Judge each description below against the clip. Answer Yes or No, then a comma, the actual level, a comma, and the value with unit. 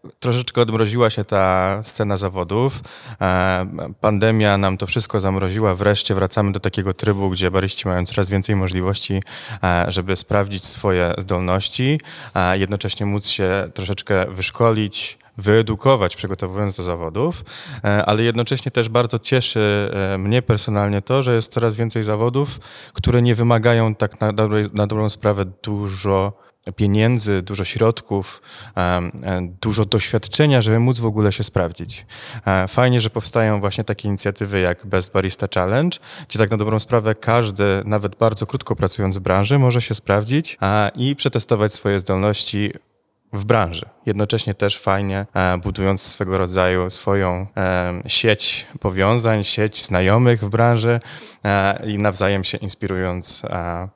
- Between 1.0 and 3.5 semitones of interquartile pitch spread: Yes, average, 3.0 semitones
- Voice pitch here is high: No, low, 105 Hz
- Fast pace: No, average, 130 wpm